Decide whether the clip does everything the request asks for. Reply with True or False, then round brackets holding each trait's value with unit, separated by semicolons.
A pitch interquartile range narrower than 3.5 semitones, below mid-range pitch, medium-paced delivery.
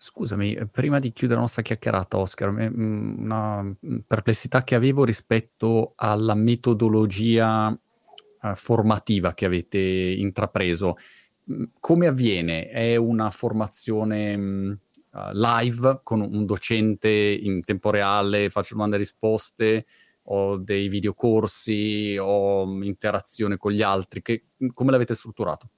False (2.4 semitones; 110 Hz; 110 wpm)